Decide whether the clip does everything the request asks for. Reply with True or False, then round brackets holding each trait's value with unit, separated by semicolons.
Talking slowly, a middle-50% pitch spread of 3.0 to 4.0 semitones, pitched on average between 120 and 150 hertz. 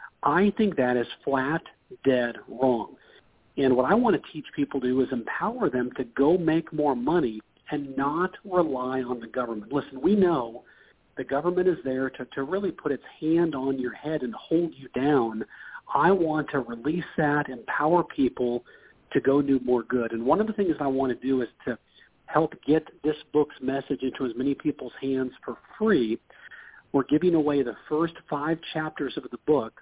False (190 wpm; 3.4 semitones; 140 Hz)